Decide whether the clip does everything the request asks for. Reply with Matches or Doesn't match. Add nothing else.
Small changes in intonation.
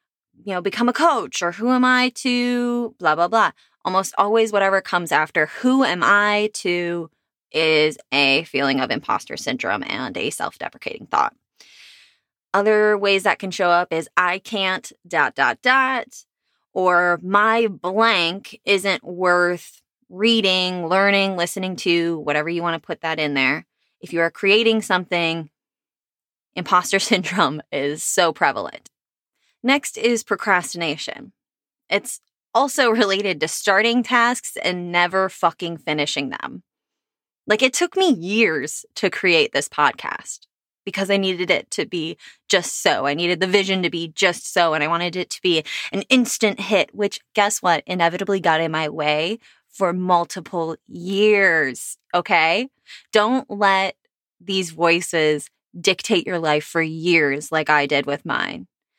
Doesn't match